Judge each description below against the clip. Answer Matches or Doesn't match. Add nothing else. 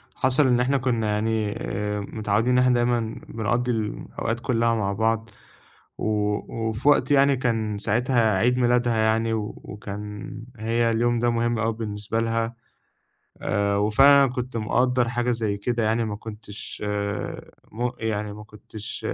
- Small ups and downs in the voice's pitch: Matches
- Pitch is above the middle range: Doesn't match